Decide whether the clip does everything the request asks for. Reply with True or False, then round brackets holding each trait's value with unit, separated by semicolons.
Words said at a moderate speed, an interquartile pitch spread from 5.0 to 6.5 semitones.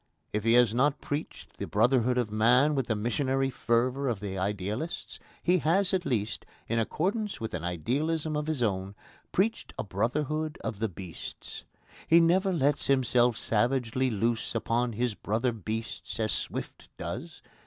True (160 wpm; 5.3 semitones)